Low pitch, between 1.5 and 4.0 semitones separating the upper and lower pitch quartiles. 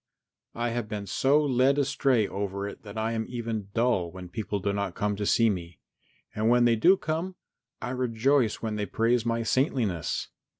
Yes: low, 115 Hz; average, 3.5 semitones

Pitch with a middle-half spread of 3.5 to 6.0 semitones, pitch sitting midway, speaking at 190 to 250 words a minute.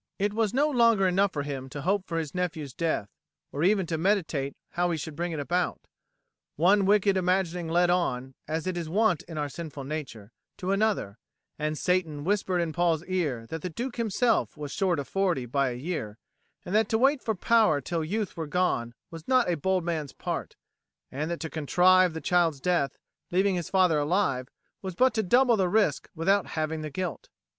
Yes: average, 4.1 semitones; medium, 175 Hz; average, 200 wpm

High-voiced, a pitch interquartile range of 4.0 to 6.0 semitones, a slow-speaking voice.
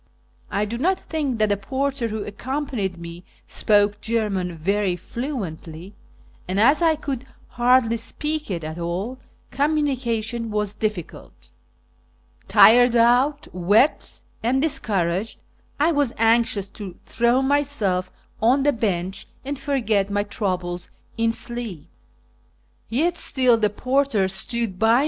Yes: high, 225 Hz; average, 5.0 semitones; slow, 130 wpm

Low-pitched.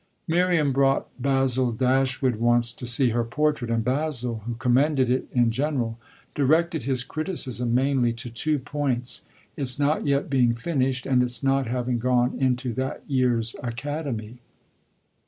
Yes: low, 130 Hz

